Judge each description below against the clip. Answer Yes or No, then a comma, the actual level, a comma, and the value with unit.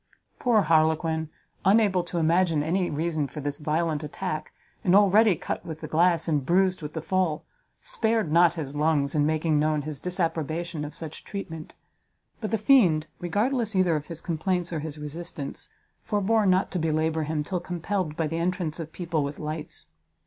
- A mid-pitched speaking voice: Yes, medium, 165 Hz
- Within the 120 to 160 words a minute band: No, average, 175 wpm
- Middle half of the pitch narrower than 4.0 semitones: Yes, average, 3.1 semitones